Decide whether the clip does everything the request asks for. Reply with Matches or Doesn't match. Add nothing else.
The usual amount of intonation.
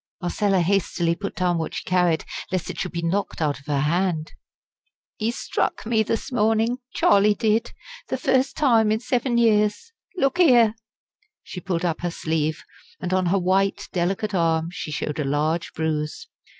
Matches